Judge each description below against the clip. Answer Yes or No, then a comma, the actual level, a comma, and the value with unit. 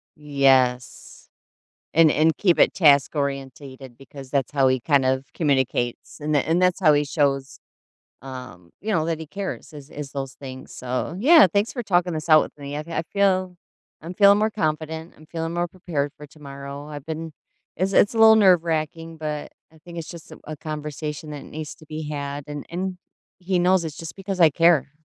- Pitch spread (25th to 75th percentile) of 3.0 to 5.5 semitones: Yes, average, 3.6 semitones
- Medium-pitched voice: Yes, medium, 155 Hz